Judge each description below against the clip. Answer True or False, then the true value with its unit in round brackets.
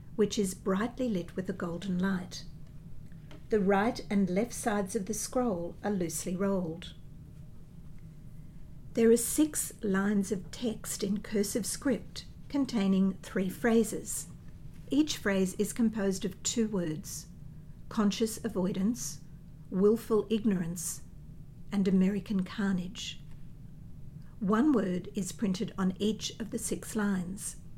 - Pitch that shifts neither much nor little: True (4.6 semitones)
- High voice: True (195 Hz)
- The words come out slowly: True (120 wpm)